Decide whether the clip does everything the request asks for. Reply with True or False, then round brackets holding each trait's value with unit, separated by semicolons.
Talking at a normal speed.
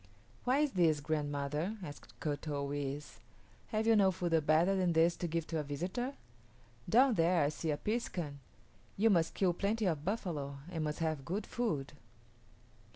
True (170 wpm)